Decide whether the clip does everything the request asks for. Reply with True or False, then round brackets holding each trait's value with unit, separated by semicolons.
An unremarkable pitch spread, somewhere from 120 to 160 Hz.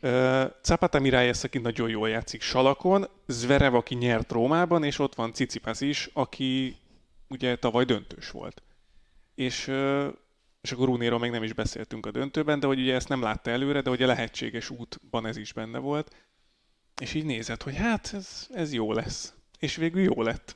True (3.5 semitones; 130 Hz)